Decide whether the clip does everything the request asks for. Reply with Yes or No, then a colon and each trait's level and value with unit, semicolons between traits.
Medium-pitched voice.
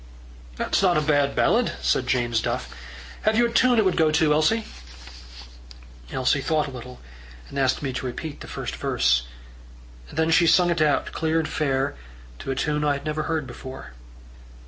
Yes: medium, 150 Hz